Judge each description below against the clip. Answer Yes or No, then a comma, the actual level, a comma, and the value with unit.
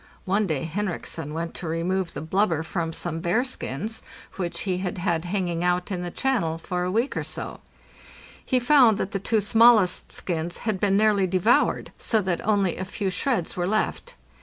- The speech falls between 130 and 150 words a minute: No, average, 185 wpm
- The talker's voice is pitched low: No, medium, 185 Hz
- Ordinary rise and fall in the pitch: Yes, average, 3.6 semitones